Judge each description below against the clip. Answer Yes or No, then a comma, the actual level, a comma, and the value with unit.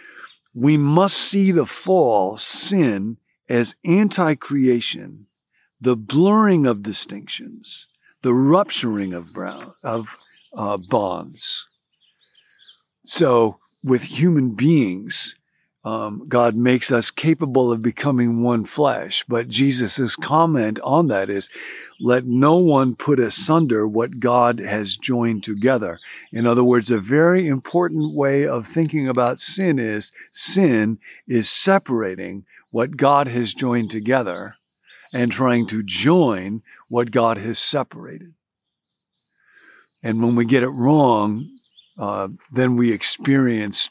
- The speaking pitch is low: Yes, low, 125 Hz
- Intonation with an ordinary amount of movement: Yes, average, 4.5 semitones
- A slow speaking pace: Yes, slow, 120 wpm